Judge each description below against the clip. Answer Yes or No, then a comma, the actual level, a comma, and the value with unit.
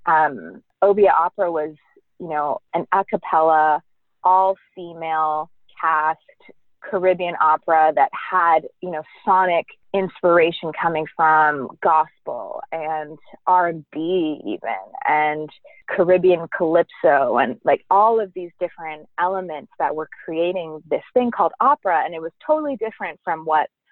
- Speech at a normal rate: No, slow, 130 wpm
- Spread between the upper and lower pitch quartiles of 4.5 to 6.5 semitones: No, average, 3.5 semitones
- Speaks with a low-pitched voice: No, medium, 170 Hz